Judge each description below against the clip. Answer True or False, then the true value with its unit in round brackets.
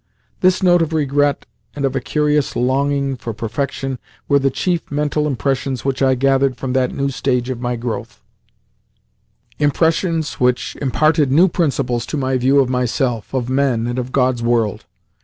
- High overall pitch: False (135 Hz)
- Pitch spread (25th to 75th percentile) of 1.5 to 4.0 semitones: True (2.5 semitones)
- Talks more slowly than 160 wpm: False (165 wpm)